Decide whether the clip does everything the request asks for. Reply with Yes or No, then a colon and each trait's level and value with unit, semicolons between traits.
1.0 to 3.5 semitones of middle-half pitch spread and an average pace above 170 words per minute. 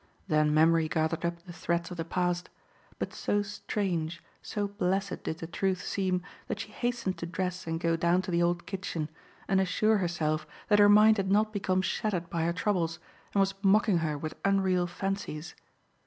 Yes: average, 2.9 semitones; average, 185 wpm